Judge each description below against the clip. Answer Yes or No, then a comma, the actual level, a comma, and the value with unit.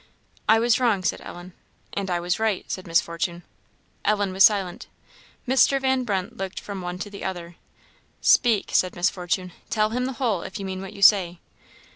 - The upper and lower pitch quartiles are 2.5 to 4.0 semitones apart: Yes, average, 3.6 semitones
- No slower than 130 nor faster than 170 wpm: No, average, 190 wpm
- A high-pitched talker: Yes, high, 195 Hz